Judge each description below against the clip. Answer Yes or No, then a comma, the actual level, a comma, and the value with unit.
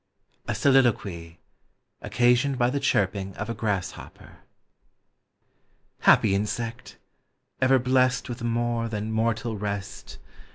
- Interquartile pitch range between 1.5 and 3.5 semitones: Yes, average, 3.2 semitones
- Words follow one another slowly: Yes, slow, 110 wpm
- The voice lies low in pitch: Yes, low, 115 Hz